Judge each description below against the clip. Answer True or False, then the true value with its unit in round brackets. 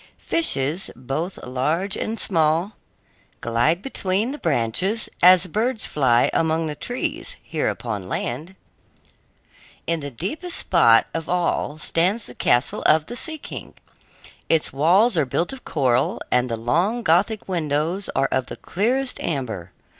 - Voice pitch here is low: False (165 Hz)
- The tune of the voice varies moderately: False (6.9 semitones)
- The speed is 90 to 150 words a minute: True (140 wpm)